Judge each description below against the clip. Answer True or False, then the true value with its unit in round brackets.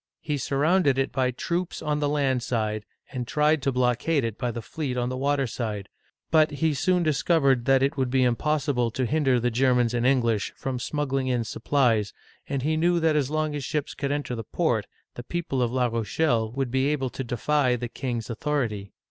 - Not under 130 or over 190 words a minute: False (205 wpm)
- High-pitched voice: False (130 Hz)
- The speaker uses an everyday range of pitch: True (3.4 semitones)